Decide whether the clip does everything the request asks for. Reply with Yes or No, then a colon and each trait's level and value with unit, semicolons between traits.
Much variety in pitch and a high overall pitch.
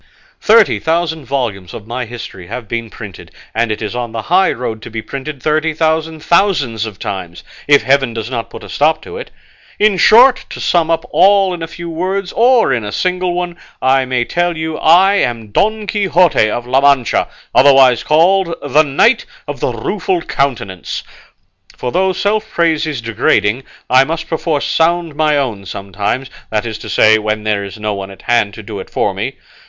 No: wide, 7.3 semitones; medium, 140 Hz